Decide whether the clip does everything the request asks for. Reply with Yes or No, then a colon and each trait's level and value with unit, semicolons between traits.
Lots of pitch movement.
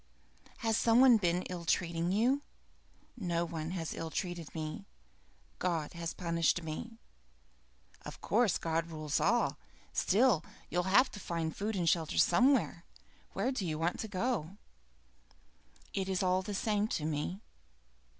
No: average, 4.4 semitones